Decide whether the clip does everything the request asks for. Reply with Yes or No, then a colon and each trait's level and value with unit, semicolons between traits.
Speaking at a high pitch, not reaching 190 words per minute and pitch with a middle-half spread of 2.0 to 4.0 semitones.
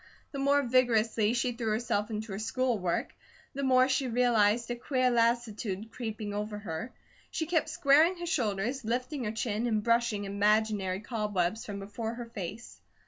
Yes: high, 230 Hz; average, 165 wpm; average, 3.1 semitones